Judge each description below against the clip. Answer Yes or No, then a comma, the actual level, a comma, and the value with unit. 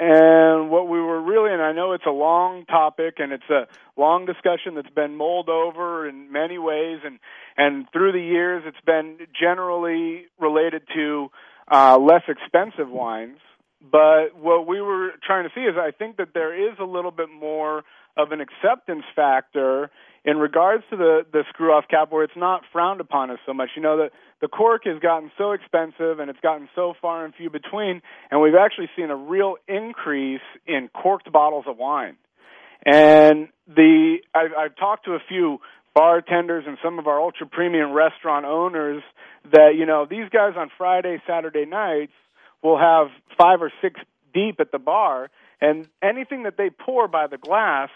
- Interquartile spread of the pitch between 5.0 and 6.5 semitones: No, average, 3.0 semitones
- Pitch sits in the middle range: Yes, medium, 165 Hz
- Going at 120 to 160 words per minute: No, average, 180 wpm